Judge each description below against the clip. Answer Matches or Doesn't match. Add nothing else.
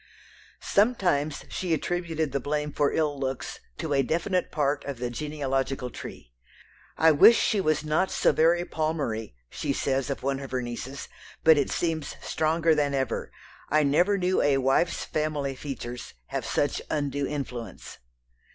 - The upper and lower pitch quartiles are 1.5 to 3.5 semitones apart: Matches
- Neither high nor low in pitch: Matches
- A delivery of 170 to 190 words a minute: Doesn't match